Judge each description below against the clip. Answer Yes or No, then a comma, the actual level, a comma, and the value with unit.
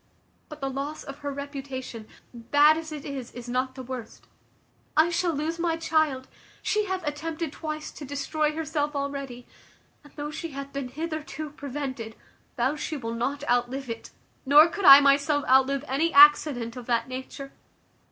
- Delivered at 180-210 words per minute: No, average, 165 wpm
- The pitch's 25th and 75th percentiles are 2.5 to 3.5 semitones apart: Yes, average, 2.9 semitones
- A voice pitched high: Yes, very high, 285 Hz